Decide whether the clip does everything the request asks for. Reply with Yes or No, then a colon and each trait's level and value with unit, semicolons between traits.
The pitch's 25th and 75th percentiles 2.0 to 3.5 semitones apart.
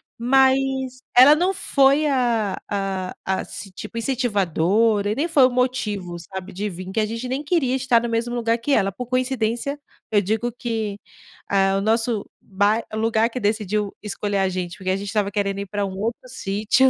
No: average, 4.2 semitones